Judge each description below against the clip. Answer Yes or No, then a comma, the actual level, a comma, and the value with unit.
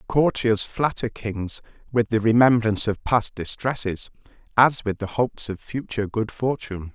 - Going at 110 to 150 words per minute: Yes, average, 145 wpm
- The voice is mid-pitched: No, low, 110 Hz